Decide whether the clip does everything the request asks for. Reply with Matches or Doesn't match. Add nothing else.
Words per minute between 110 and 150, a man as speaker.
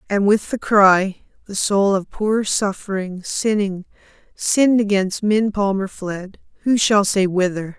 Doesn't match